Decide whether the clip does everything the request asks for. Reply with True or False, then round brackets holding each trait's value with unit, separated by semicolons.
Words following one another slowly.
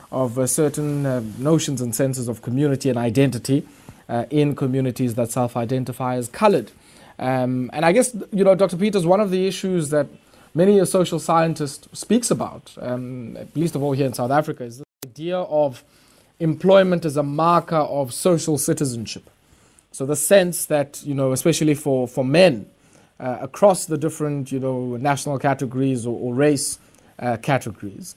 False (170 wpm)